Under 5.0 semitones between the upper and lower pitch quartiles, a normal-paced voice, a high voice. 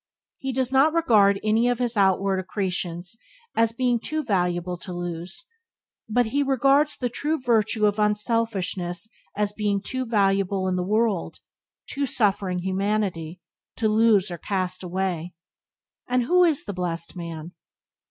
Yes: average, 4.6 semitones; average, 150 wpm; high, 205 Hz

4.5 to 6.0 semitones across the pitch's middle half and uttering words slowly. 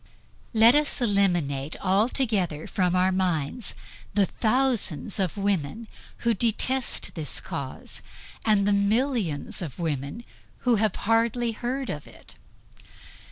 Yes: average, 5.1 semitones; slow, 115 wpm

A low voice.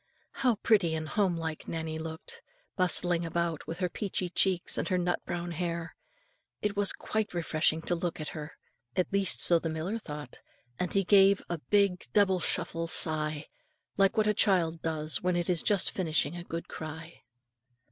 No: medium, 175 Hz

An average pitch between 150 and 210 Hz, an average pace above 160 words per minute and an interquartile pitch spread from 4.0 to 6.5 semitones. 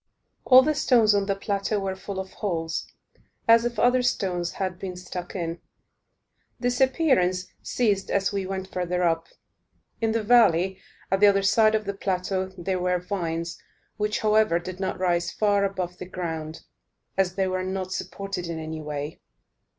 No: high, 190 Hz; average, 170 wpm; average, 2.7 semitones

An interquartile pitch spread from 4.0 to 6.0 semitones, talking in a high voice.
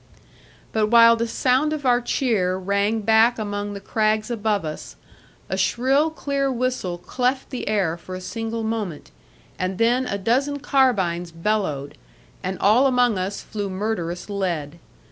Yes: average, 4.6 semitones; high, 215 Hz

